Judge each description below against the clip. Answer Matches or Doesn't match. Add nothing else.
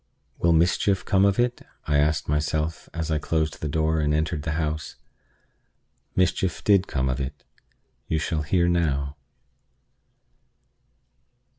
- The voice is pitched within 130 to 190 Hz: Doesn't match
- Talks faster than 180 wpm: Doesn't match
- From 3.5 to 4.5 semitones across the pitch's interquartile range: Doesn't match